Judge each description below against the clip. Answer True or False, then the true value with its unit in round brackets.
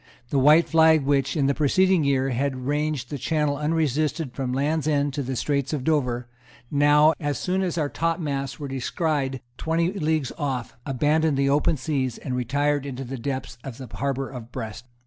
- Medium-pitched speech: True (145 Hz)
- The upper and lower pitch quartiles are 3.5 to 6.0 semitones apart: False (2.7 semitones)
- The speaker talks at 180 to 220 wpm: True (185 wpm)